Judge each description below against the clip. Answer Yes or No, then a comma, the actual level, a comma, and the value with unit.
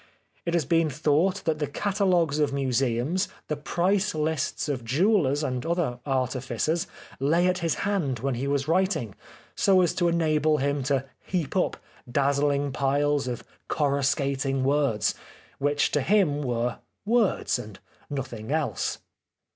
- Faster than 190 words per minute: No, average, 140 wpm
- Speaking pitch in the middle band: Yes, medium, 145 Hz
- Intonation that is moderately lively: Yes, average, 4.0 semitones